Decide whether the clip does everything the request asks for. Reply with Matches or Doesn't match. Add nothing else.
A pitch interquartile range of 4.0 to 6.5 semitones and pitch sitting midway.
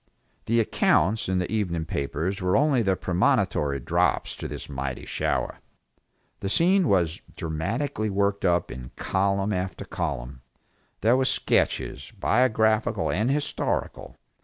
Doesn't match